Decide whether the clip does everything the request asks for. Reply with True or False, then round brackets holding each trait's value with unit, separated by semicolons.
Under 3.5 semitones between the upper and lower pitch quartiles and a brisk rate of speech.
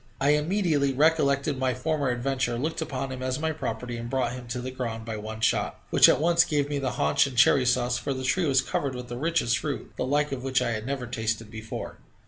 True (3.1 semitones; 240 wpm)